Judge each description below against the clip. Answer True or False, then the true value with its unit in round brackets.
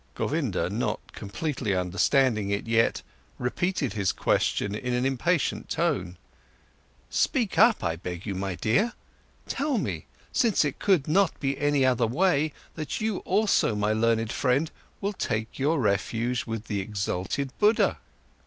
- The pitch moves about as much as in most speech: False (7.8 semitones)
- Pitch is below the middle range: True (125 Hz)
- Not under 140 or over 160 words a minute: True (145 wpm)